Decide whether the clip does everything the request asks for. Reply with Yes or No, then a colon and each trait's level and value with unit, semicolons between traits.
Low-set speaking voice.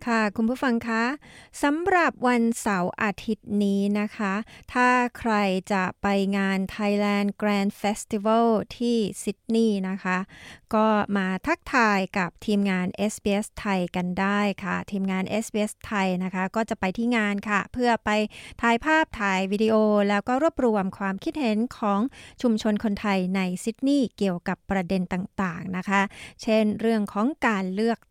No: high, 210 Hz